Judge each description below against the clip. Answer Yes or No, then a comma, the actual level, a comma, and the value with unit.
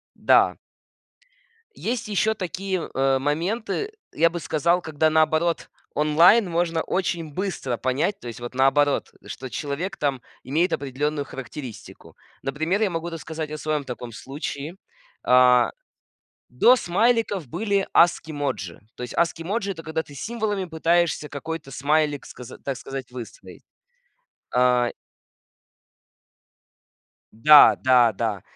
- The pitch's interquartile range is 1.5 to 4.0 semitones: No, average, 4.7 semitones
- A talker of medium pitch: Yes, medium, 155 Hz